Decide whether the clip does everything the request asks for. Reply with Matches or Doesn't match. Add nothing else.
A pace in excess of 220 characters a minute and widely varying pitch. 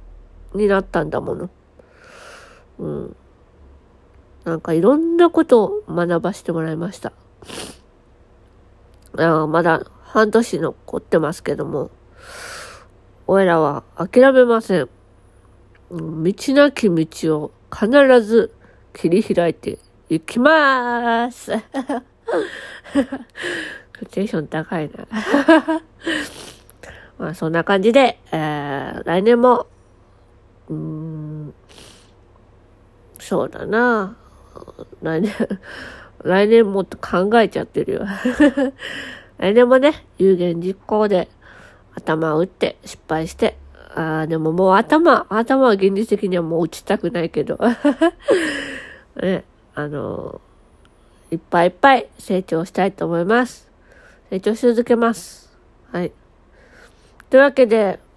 Doesn't match